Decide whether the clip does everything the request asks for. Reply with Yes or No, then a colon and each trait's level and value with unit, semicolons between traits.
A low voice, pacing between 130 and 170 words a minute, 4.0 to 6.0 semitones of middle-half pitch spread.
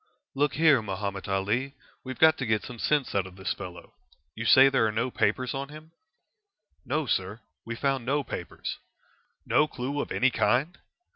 No: low, 125 Hz; average, 180 wpm; average, 4.6 semitones